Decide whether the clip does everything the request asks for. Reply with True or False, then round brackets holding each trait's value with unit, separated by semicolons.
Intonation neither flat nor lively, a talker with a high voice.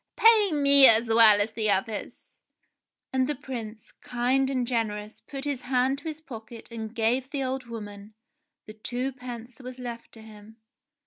True (3.3 semitones; 240 Hz)